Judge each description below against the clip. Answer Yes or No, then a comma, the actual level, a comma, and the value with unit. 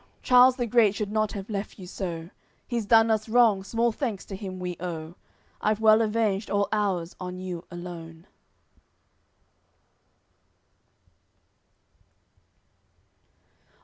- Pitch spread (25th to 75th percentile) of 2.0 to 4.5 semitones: Yes, average, 3.6 semitones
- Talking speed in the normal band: No, slow, 115 wpm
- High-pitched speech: Yes, high, 205 Hz